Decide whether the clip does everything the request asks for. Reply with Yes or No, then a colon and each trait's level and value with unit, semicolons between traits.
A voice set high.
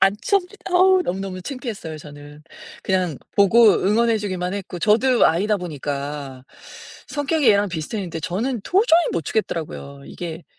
Yes: high, 195 Hz